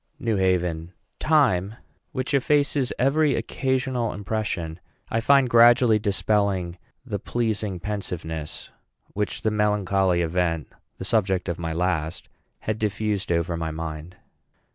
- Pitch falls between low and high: No, low, 100 Hz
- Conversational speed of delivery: No, slow, 120 wpm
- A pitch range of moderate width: Yes, average, 4.7 semitones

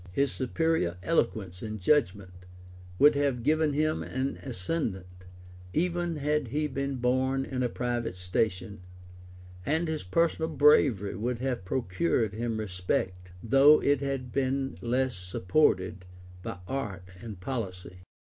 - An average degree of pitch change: No, wide, 7.1 semitones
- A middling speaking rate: No, slow, 130 wpm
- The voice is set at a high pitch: No, low, 125 Hz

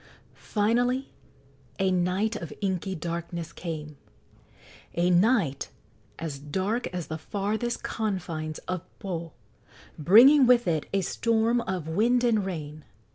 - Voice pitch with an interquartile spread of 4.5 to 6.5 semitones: Yes, average, 5.1 semitones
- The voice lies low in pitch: No, medium, 185 Hz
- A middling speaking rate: No, slow, 120 wpm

